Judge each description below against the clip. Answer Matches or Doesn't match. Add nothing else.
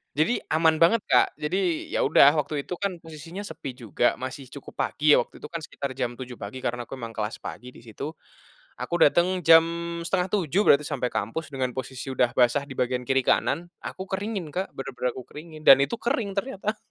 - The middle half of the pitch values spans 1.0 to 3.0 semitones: Doesn't match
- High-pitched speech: Doesn't match